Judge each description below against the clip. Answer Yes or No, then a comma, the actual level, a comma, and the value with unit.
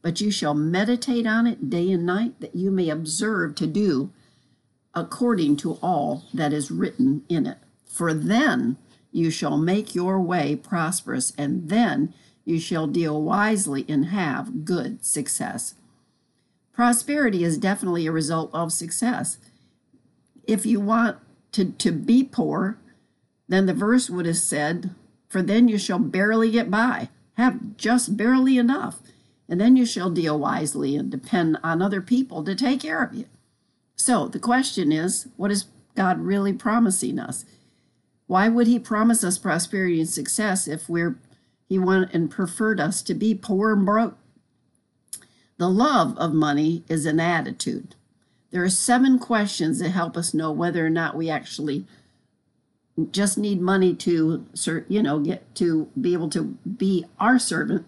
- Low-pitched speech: No, high, 190 Hz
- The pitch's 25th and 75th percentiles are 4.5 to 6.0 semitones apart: Yes, wide, 5.6 semitones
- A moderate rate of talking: Yes, average, 160 wpm